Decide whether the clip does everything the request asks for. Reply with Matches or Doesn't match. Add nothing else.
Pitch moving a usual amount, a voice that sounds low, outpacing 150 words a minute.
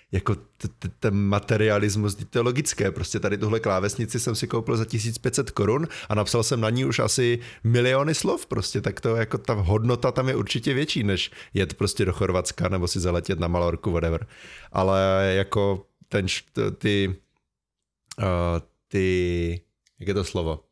Matches